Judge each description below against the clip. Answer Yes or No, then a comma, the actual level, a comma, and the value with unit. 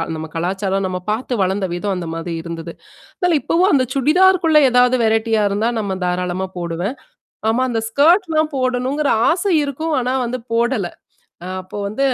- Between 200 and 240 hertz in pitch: Yes, high, 230 Hz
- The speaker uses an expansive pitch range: Yes, wide, 7.2 semitones